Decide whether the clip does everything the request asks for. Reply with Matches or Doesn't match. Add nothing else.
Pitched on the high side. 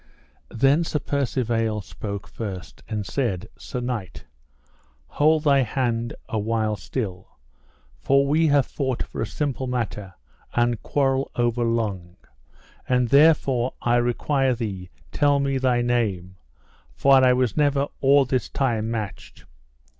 Doesn't match